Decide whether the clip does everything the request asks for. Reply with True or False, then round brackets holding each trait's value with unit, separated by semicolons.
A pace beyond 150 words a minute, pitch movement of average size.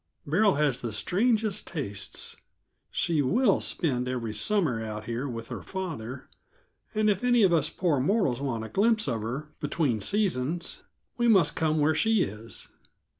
False (160 wpm; 8.2 semitones)